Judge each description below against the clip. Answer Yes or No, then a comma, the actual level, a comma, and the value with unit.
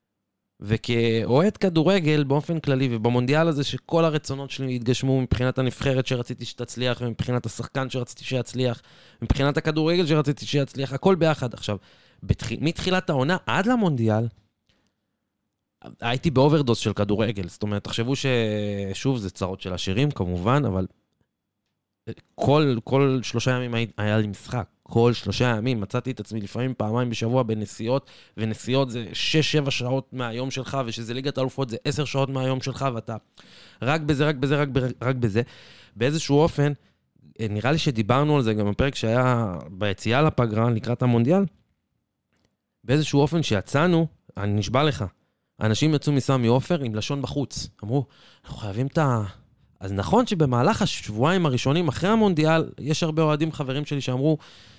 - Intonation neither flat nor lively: Yes, average, 4.4 semitones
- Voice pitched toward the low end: Yes, low, 130 Hz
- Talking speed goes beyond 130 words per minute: Yes, average, 140 wpm